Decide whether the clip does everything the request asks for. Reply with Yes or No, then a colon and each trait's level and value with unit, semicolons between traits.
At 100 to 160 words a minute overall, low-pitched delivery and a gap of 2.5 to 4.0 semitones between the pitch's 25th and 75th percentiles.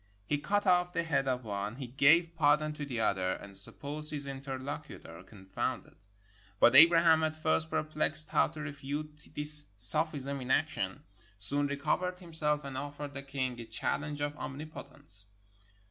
No: average, 155 wpm; medium, 145 Hz; average, 2.8 semitones